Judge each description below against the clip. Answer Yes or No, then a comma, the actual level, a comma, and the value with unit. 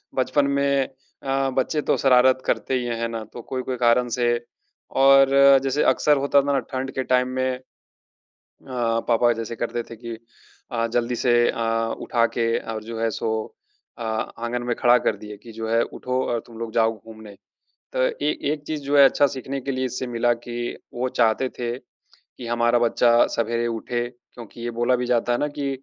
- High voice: No, low, 120 Hz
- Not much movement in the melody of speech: Yes, narrow, 2.1 semitones